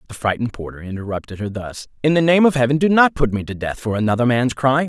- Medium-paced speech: No, fast, 260 wpm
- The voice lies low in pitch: Yes, low, 125 Hz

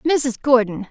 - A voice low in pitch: No, high, 245 Hz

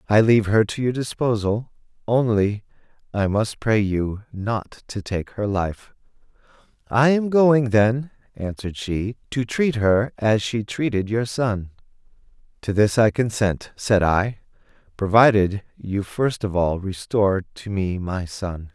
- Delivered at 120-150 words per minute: Yes, average, 145 wpm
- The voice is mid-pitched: No, low, 105 Hz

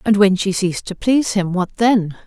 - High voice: Yes, high, 200 Hz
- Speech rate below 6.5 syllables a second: Yes, 5.3 syllables/s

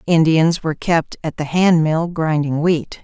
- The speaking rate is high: No, average, 160 wpm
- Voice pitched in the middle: Yes, medium, 160 Hz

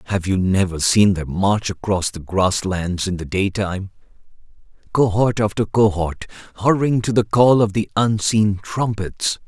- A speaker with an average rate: Yes, average, 150 wpm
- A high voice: No, low, 100 Hz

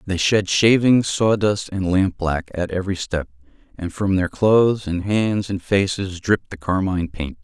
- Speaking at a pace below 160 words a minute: No, average, 170 wpm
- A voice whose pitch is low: Yes, very low, 95 Hz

